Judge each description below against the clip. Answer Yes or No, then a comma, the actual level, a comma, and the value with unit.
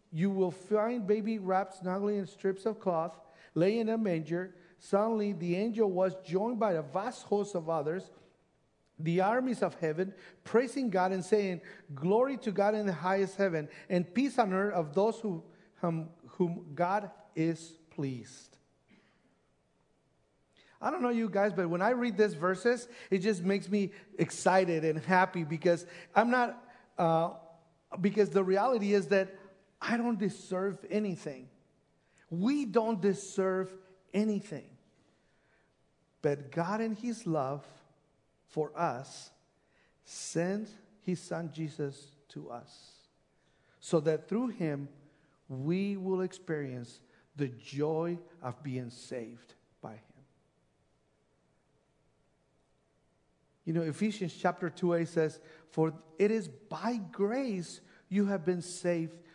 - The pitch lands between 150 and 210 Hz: Yes, medium, 185 Hz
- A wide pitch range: No, average, 3.9 semitones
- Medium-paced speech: No, slow, 130 wpm